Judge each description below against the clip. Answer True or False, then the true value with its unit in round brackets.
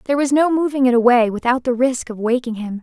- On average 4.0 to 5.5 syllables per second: False (6.4 syllables/s)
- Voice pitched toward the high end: True (250 Hz)